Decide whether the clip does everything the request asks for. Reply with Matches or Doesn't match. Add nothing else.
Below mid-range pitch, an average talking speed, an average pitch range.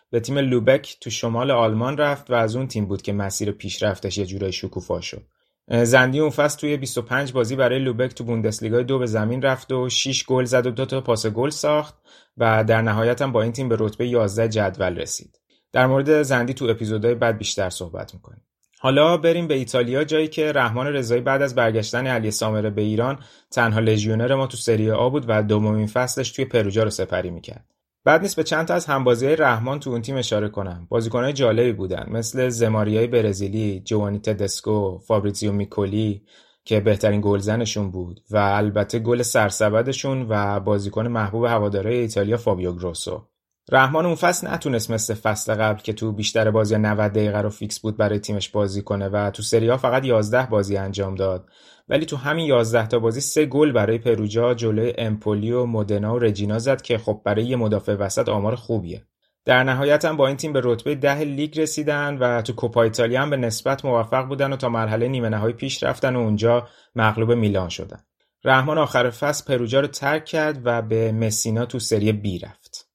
Doesn't match